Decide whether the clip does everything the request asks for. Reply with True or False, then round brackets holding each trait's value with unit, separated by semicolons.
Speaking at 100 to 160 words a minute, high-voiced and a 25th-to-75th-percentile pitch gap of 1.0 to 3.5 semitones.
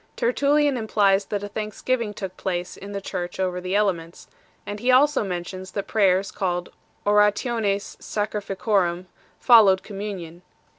True (155 wpm; 200 Hz; 2.5 semitones)